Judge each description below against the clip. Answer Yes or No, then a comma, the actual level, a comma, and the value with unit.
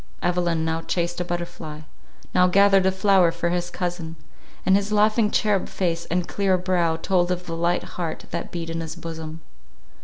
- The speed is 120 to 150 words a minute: No, average, 175 wpm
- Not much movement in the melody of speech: Yes, narrow, 2.1 semitones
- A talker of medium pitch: Yes, medium, 175 Hz